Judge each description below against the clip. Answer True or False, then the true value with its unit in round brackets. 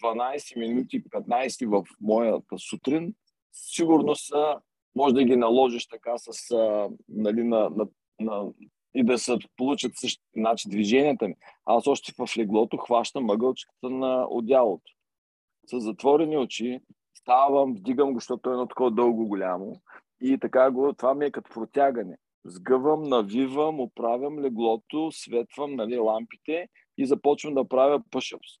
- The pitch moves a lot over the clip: False (3.5 semitones)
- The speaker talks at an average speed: True (140 wpm)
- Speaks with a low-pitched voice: True (125 Hz)